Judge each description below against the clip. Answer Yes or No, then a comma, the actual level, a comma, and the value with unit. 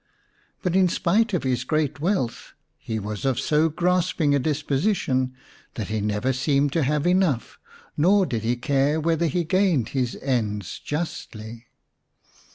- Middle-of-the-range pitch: Yes, medium, 145 Hz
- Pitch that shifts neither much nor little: No, wide, 5.8 semitones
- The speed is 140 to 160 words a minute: Yes, average, 150 wpm